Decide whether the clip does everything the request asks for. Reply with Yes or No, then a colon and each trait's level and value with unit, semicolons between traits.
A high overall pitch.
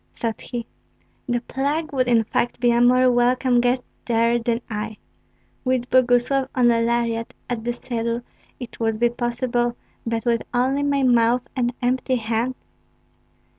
Yes: high, 240 Hz